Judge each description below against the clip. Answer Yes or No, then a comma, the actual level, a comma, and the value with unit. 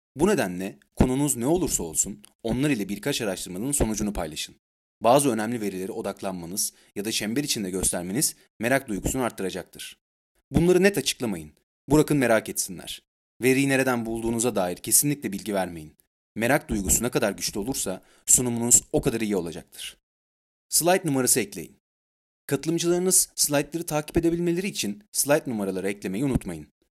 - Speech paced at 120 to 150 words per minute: Yes, average, 135 wpm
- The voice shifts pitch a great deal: Yes, wide, 6.9 semitones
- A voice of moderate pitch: No, low, 115 Hz